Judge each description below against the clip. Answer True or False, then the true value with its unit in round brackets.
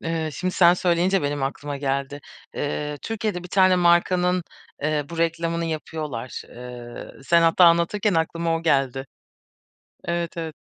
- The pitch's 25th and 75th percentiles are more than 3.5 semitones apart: False (3.2 semitones)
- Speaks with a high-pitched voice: False (165 Hz)